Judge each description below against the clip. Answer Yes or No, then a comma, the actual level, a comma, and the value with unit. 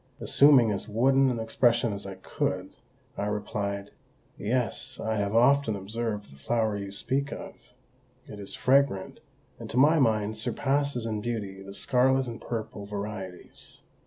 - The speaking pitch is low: Yes, low, 110 Hz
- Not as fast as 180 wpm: Yes, average, 150 wpm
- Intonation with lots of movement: No, average, 3.8 semitones